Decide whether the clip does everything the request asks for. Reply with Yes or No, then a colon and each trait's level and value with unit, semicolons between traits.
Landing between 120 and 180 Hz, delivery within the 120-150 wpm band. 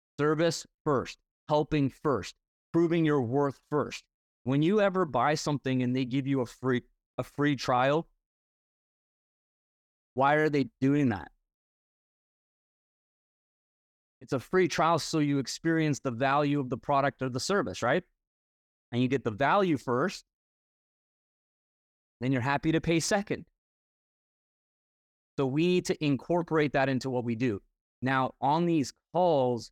Yes: medium, 140 Hz; average, 140 wpm